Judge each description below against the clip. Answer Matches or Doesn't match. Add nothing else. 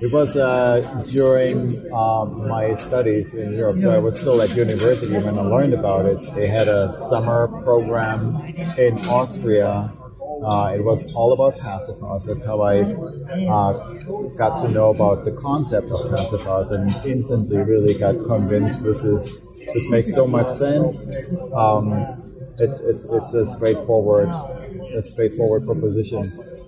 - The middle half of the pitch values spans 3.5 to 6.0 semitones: Matches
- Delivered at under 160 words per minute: Matches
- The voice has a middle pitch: Doesn't match